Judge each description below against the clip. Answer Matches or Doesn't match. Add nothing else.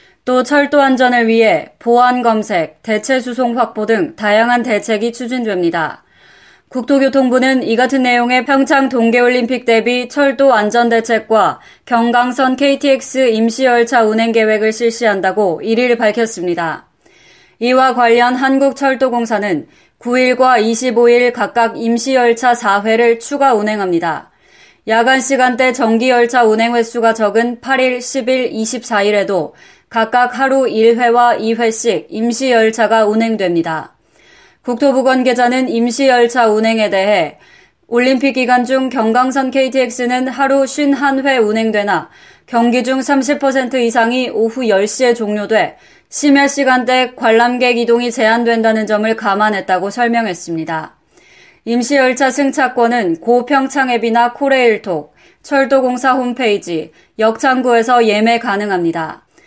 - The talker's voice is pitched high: Matches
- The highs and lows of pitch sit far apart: Doesn't match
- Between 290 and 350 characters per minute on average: Doesn't match